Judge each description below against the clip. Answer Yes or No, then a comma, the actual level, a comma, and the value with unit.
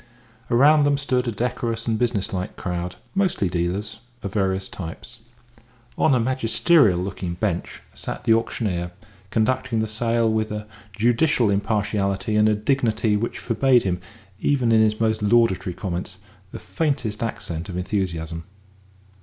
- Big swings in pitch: No, average, 3.7 semitones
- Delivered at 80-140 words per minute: Yes, slow, 135 wpm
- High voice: No, low, 110 Hz